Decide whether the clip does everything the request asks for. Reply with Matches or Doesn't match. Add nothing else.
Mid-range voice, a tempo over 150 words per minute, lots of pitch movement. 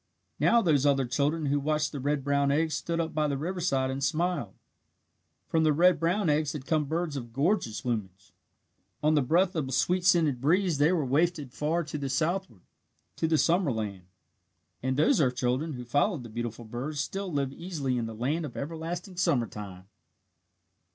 Doesn't match